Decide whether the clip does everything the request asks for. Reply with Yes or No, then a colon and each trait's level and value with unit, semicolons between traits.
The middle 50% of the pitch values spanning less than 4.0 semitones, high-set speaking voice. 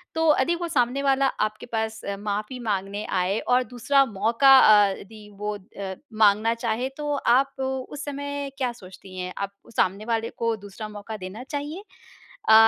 No: average, 4.8 semitones; high, 225 Hz